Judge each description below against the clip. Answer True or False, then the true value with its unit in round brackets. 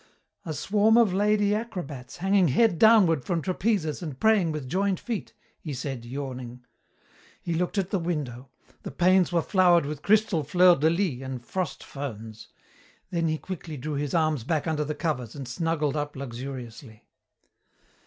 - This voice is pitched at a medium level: True (160 Hz)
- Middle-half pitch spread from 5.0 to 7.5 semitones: True (5.4 semitones)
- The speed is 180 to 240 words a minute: False (165 wpm)